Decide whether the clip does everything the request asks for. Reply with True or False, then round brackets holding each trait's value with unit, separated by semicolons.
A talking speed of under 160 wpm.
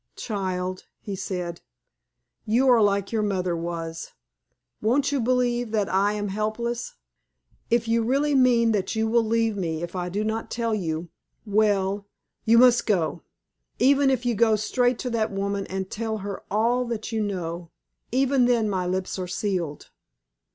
False (165 wpm)